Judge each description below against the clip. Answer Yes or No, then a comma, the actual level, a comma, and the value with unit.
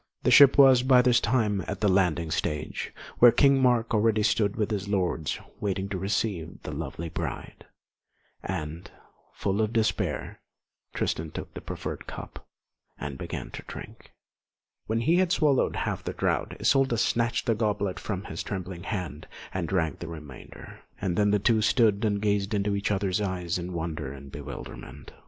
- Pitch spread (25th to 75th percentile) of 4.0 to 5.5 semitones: Yes, average, 4.6 semitones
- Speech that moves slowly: No, average, 170 wpm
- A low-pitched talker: Yes, low, 100 Hz